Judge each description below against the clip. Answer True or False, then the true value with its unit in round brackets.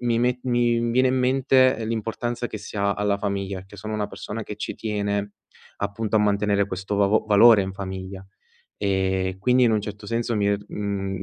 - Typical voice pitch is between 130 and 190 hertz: False (105 Hz)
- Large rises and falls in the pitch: False (2.6 semitones)